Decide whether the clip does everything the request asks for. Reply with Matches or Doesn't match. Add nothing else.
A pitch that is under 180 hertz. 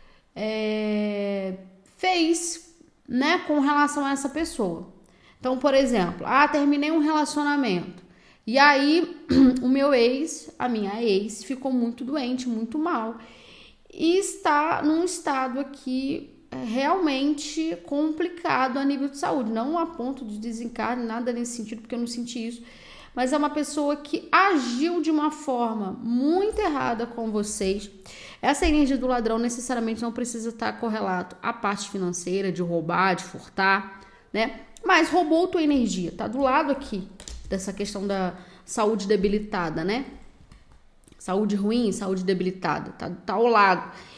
Doesn't match